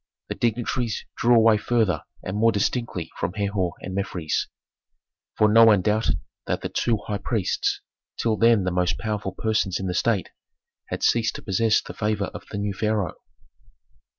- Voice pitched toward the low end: Yes, low, 105 Hz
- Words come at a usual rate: Yes, average, 170 wpm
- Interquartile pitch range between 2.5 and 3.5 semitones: Yes, average, 2.9 semitones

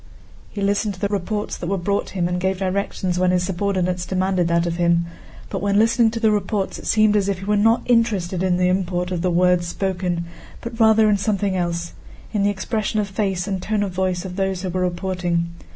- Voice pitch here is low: No, high, 190 Hz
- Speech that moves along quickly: Yes, fast, 220 wpm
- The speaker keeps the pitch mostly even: Yes, narrow, 2.3 semitones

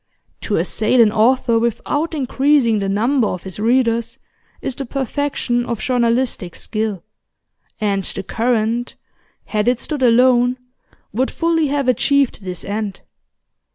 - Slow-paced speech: Yes, slow, 130 wpm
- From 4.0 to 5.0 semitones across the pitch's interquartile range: No, average, 3.4 semitones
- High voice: Yes, high, 235 Hz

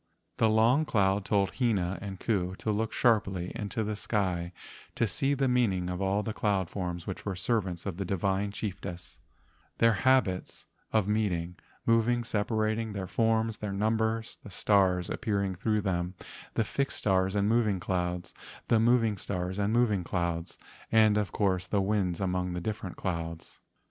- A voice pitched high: No, low, 100 Hz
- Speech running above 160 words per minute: Yes, average, 170 wpm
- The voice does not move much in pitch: No, average, 3.2 semitones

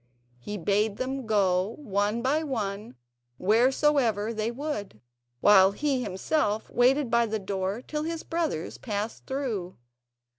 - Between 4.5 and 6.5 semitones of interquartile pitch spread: Yes, average, 4.8 semitones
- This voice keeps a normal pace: No, slow, 125 wpm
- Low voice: No, high, 220 Hz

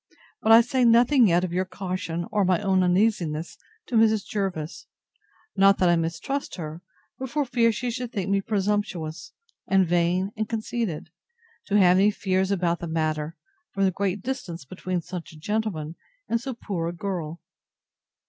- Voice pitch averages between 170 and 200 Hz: Yes, high, 190 Hz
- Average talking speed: Yes, average, 170 wpm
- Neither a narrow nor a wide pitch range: Yes, average, 4.2 semitones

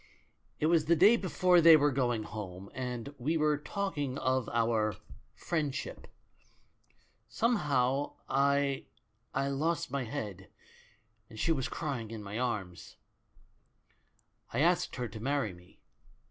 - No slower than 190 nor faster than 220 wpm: No, slow, 135 wpm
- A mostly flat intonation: No, average, 5.2 semitones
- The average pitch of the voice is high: No, low, 135 Hz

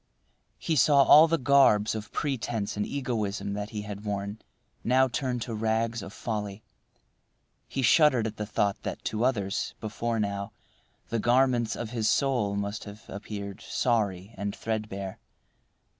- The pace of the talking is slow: No, average, 150 wpm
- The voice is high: No, low, 110 Hz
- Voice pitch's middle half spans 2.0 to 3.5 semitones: Yes, average, 3.1 semitones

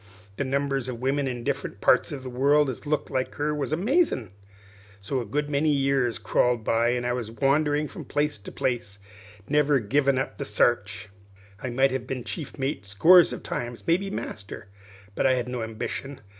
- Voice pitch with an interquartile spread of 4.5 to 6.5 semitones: No, average, 3.4 semitones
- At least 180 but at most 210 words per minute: Yes, average, 185 wpm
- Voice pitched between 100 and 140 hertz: Yes, low, 135 Hz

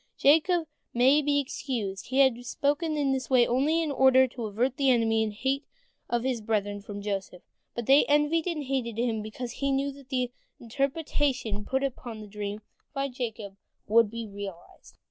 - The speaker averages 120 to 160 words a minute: No, average, 185 wpm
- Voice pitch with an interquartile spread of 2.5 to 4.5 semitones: Yes, average, 4.1 semitones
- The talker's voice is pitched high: Yes, very high, 250 Hz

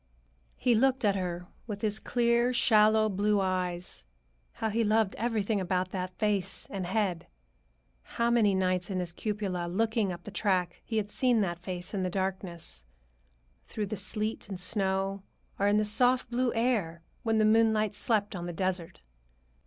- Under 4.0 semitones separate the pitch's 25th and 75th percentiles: Yes, average, 3.2 semitones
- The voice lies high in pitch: Yes, high, 205 Hz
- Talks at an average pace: Yes, average, 170 wpm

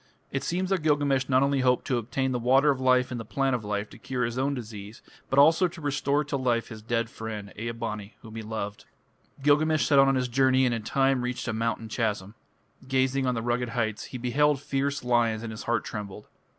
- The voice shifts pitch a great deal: No, average, 3.3 semitones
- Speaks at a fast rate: Yes, fast, 230 wpm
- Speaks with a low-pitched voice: Yes, low, 125 Hz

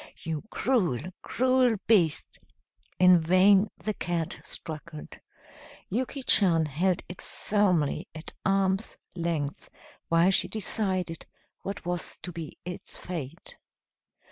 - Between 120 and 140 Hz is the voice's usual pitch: No, medium, 180 Hz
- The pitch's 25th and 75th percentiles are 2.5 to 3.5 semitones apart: Yes, average, 3.2 semitones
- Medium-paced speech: No, slow, 110 wpm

